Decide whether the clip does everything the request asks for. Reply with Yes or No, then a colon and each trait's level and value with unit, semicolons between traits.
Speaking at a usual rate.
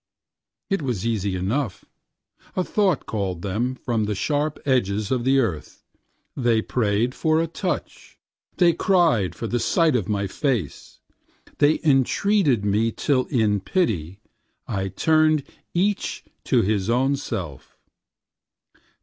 No: slow, 130 wpm